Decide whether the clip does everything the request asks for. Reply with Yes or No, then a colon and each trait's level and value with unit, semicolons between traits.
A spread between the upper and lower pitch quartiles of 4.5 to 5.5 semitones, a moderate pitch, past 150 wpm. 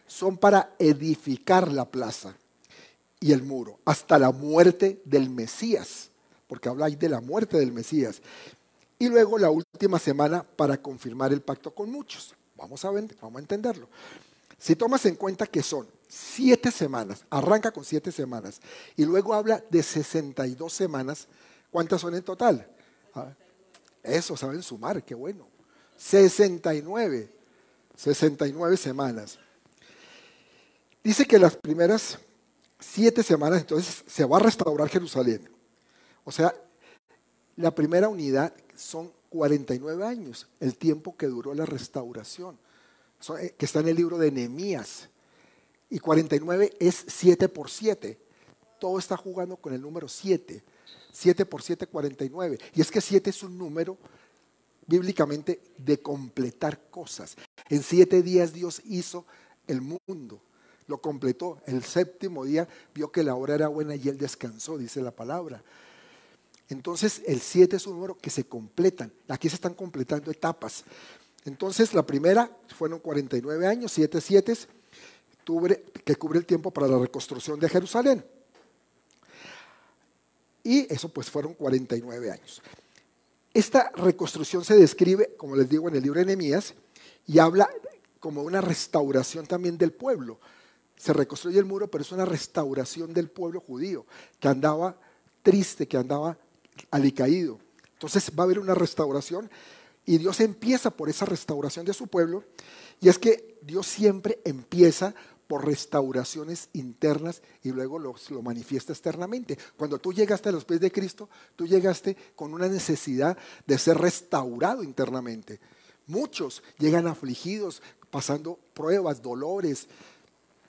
No: average, 4.9 semitones; medium, 165 Hz; average, 140 wpm